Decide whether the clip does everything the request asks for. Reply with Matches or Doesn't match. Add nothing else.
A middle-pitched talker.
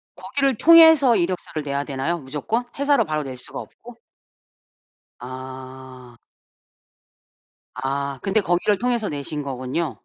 Matches